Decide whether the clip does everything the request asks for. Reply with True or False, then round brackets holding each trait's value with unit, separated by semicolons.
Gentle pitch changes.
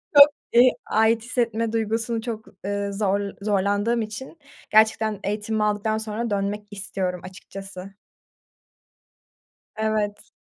True (1.8 semitones)